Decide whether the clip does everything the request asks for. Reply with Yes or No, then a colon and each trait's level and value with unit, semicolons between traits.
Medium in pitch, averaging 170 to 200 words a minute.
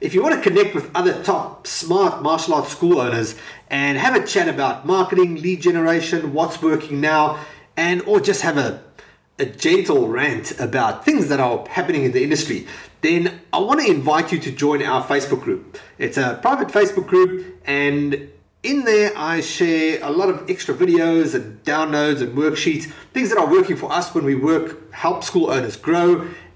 Yes: medium, 170 Hz; average, 190 wpm